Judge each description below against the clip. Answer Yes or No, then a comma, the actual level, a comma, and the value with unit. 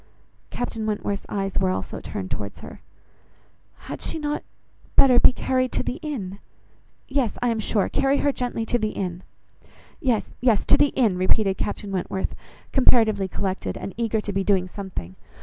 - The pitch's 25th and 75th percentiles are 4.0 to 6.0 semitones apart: Yes, average, 4.4 semitones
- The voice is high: Yes, high, 215 Hz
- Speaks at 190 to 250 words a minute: No, average, 165 wpm